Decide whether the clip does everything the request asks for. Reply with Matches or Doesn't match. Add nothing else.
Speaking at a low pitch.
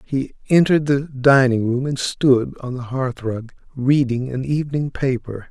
Matches